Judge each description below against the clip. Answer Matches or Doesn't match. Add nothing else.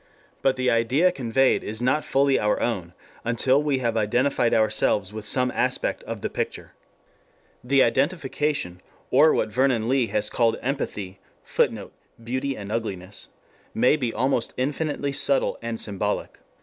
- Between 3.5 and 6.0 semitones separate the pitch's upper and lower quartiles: Matches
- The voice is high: Doesn't match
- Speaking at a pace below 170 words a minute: Matches